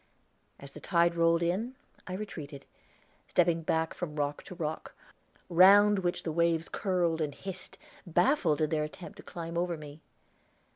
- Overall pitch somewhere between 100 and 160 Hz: No, medium, 170 Hz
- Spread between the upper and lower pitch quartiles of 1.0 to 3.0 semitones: Yes, narrow, 2.6 semitones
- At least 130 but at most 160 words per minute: Yes, average, 155 wpm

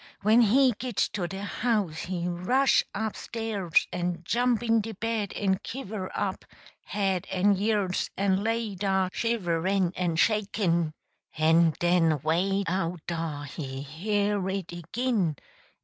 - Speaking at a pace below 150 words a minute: Yes, slow, 135 wpm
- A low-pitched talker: No, high, 190 Hz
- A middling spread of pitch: Yes, average, 3.9 semitones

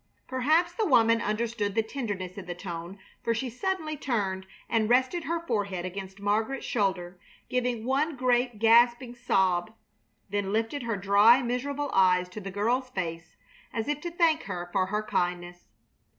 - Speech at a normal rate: Yes, average, 160 wpm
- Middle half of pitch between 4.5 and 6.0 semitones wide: Yes, average, 4.9 semitones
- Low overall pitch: No, high, 225 Hz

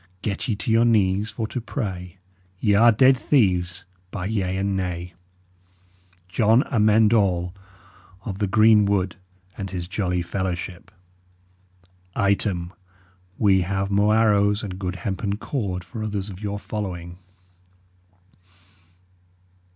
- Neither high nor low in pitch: No, low, 100 Hz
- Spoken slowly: Yes, slow, 125 wpm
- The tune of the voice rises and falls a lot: No, average, 2.8 semitones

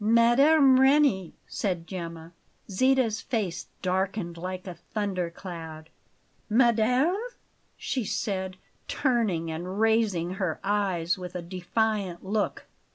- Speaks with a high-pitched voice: Yes, high, 195 Hz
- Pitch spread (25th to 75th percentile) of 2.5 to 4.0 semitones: No, average, 4.4 semitones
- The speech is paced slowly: Yes, slow, 105 wpm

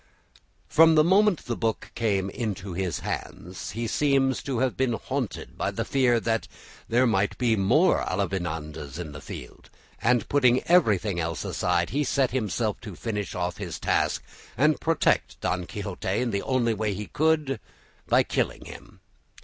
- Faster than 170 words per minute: No, average, 165 wpm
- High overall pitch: No, low, 115 Hz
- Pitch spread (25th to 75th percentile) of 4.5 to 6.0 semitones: Yes, wide, 5.6 semitones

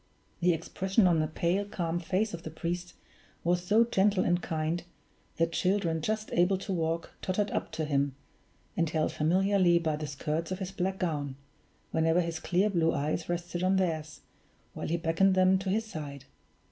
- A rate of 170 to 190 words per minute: Yes, average, 180 wpm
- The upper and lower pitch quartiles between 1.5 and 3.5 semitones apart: Yes, average, 2.8 semitones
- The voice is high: No, medium, 175 Hz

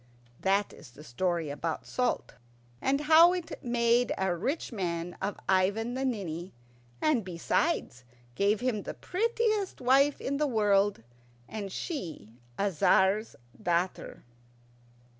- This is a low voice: No, high, 205 Hz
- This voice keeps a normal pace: No, slow, 125 wpm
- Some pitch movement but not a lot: No, wide, 6.9 semitones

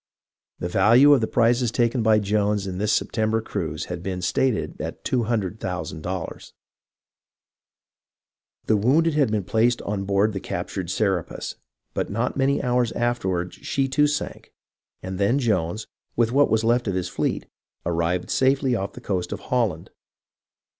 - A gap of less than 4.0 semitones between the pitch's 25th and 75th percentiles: No, average, 4.5 semitones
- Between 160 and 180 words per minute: No, average, 150 wpm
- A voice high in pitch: No, low, 110 Hz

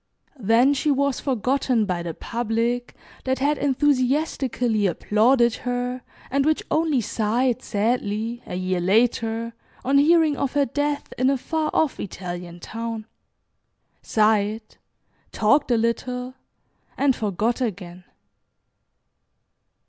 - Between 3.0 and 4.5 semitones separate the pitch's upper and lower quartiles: Yes, average, 4.1 semitones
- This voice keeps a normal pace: No, slow, 115 wpm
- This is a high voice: Yes, high, 240 Hz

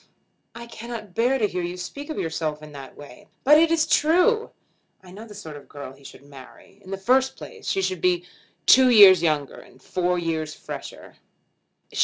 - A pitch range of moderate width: No, wide, 7.8 semitones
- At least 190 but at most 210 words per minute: Yes, average, 195 wpm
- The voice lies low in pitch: No, medium, 185 Hz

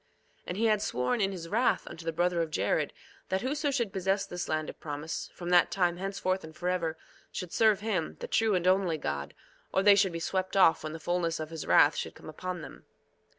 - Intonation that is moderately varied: Yes, average, 3.2 semitones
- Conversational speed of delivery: No, fast, 230 wpm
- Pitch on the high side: No, medium, 180 Hz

